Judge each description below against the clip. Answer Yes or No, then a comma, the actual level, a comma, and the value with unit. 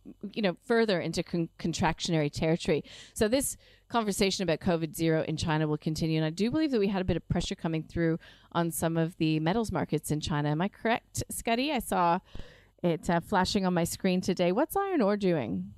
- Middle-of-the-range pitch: Yes, medium, 170 Hz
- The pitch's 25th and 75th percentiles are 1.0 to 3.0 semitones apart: No, average, 3.8 semitones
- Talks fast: Yes, fast, 210 wpm